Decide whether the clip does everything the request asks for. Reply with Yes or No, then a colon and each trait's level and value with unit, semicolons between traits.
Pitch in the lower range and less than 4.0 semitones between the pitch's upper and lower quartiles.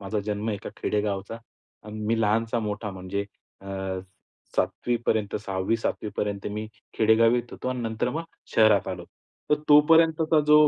Yes: low, 110 Hz; average, 2.8 semitones